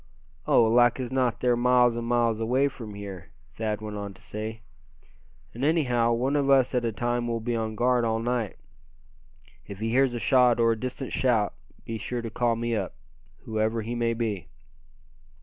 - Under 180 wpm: No, average, 190 wpm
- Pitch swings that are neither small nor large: No, narrow, 1.9 semitones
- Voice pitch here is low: Yes, low, 115 Hz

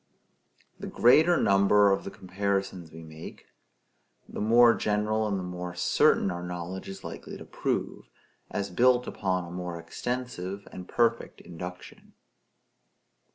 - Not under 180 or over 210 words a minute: No, slow, 135 wpm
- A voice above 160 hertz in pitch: No, very low, 95 Hz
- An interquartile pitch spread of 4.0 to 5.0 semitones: No, average, 3.2 semitones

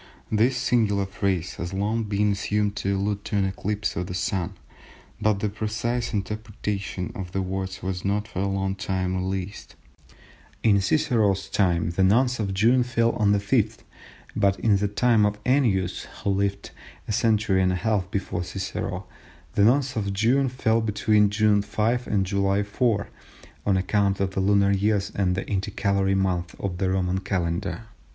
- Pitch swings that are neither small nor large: No, narrow, 2.0 semitones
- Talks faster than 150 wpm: Yes, average, 170 wpm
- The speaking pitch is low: Yes, low, 100 Hz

